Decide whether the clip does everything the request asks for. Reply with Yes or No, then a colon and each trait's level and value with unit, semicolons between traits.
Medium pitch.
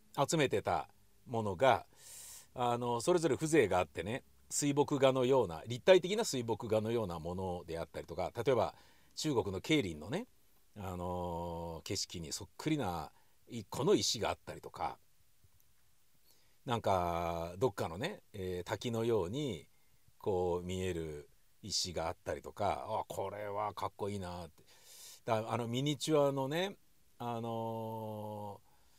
No: low, 110 Hz